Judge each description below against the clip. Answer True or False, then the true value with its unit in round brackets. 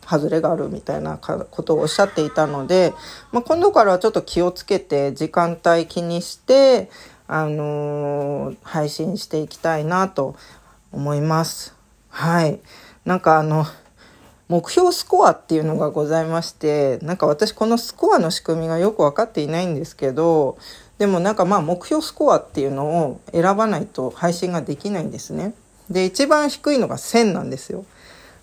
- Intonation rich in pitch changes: False (4.6 semitones)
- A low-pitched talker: False (170 Hz)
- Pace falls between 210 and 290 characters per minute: False (300 characters per minute)